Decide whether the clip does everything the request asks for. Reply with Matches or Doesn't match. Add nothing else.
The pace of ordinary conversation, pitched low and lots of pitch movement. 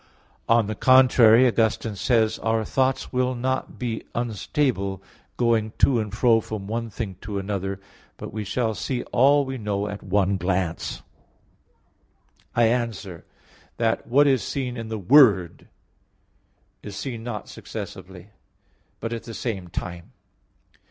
Doesn't match